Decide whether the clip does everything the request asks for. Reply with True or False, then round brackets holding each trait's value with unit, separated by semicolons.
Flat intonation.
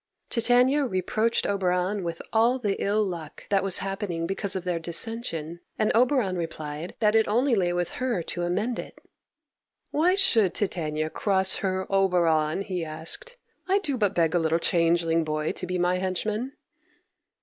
False (4.6 semitones)